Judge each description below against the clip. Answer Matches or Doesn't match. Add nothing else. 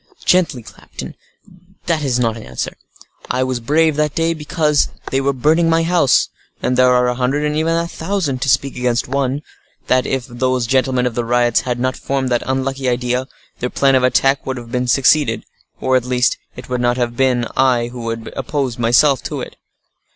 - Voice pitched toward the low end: Matches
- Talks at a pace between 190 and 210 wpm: Matches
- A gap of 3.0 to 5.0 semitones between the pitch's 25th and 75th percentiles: Doesn't match